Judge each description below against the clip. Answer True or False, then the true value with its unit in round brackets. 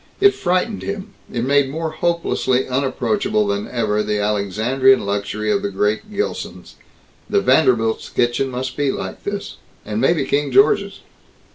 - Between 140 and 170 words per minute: True (145 wpm)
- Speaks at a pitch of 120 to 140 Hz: True (135 Hz)